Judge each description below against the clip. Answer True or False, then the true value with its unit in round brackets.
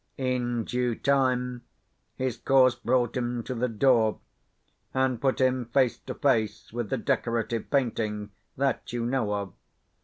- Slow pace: False (145 wpm)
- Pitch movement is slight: True (2.0 semitones)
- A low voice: True (125 Hz)